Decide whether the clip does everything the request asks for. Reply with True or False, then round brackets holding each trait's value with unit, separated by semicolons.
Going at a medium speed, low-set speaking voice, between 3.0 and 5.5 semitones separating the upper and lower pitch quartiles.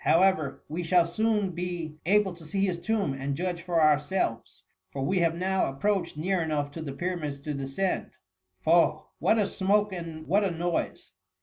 False (180 wpm; 170 Hz; 3.7 semitones)